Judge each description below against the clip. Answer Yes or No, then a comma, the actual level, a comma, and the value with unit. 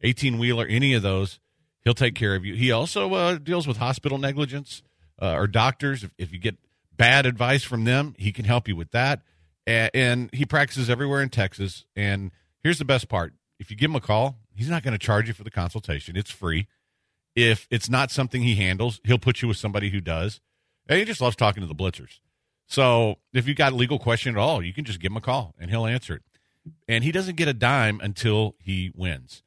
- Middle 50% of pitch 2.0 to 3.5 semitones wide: No, average, 4.7 semitones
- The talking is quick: Yes, fast, 230 wpm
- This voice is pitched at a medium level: No, low, 115 Hz